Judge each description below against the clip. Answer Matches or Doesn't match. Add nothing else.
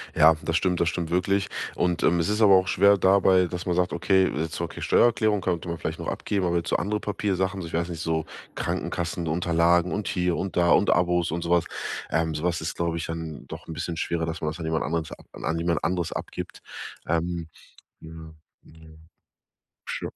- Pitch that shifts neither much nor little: Doesn't match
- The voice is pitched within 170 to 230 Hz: Doesn't match